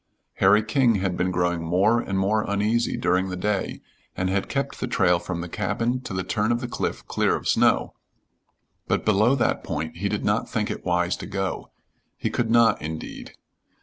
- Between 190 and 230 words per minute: Yes, average, 195 wpm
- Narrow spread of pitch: No, average, 4.0 semitones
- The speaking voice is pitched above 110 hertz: No, low, 100 Hz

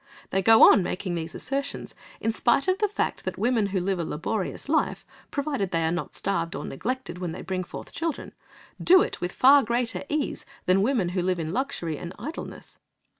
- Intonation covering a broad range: Yes, wide, 7.5 semitones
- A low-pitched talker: No, high, 200 Hz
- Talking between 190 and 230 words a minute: Yes, average, 200 wpm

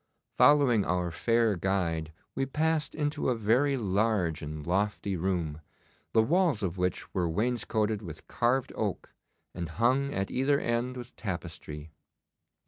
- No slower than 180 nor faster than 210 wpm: No, slow, 135 wpm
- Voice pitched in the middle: No, low, 105 Hz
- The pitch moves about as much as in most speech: No, wide, 6.4 semitones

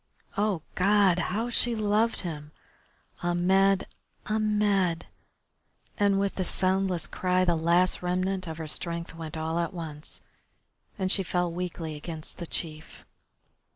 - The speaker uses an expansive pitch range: No, average, 2.9 semitones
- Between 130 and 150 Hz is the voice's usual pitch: No, medium, 180 Hz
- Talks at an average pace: No, slow, 130 wpm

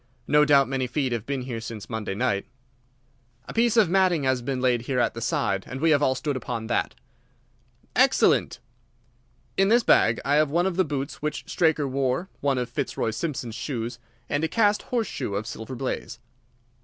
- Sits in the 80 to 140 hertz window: Yes, low, 135 Hz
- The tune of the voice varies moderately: Yes, average, 5.0 semitones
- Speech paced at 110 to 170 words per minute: No, average, 190 wpm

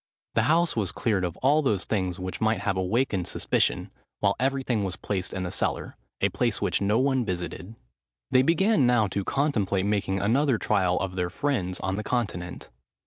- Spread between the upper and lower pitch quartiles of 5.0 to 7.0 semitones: Yes, wide, 5.6 semitones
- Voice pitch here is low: Yes, low, 105 Hz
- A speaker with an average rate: Yes, average, 180 wpm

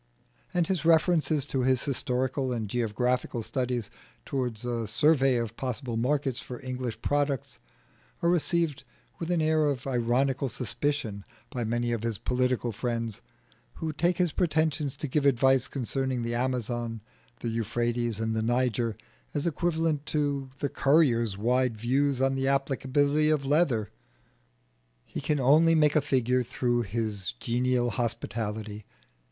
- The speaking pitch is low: Yes, low, 130 Hz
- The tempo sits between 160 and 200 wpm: No, average, 140 wpm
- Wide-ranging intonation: No, average, 3.6 semitones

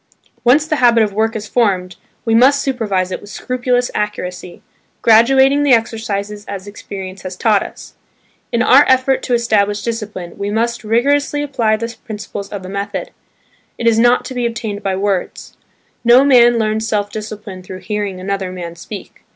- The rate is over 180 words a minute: No, average, 170 wpm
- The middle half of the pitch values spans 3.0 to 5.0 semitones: Yes, average, 3.3 semitones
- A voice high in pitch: Yes, high, 220 Hz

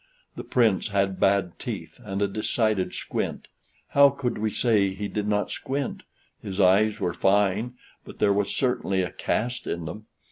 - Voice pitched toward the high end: No, low, 105 Hz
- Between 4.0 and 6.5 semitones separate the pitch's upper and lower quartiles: No, narrow, 2.4 semitones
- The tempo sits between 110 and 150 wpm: No, average, 170 wpm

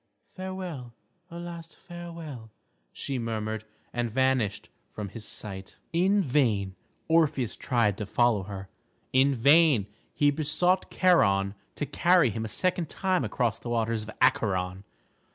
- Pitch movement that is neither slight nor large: No, wide, 7.5 semitones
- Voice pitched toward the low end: Yes, low, 125 Hz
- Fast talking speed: No, slow, 135 wpm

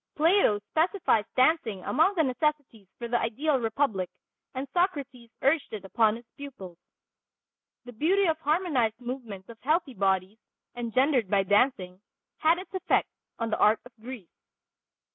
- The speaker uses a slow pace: No, average, 145 wpm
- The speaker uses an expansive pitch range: Yes, wide, 6.2 semitones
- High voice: Yes, very high, 250 Hz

